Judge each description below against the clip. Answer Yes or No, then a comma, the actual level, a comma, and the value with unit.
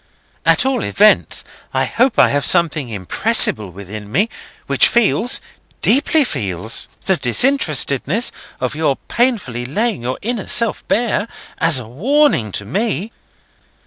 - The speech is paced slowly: Yes, slow, 120 wpm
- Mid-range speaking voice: Yes, medium, 165 Hz